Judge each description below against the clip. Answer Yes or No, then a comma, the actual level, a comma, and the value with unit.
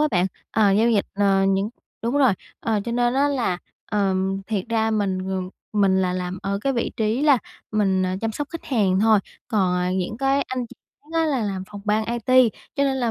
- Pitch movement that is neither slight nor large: Yes, average, 4.2 semitones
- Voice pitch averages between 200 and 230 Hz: Yes, high, 215 Hz